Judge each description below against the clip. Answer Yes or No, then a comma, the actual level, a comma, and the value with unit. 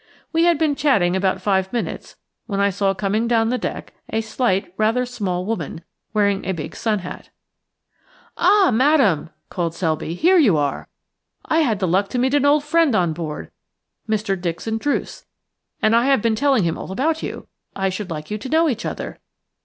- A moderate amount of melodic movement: No, wide, 6.0 semitones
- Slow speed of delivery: No, average, 195 wpm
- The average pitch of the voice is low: No, high, 215 Hz